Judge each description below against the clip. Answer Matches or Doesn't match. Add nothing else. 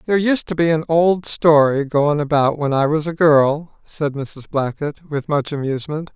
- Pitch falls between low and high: Matches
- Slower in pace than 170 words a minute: Doesn't match